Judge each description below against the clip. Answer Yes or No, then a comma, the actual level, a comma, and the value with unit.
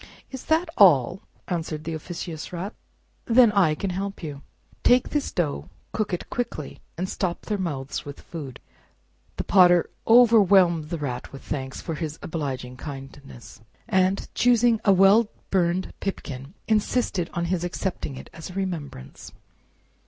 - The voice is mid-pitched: Yes, medium, 175 Hz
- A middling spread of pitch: Yes, average, 5.0 semitones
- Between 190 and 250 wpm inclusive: No, average, 150 wpm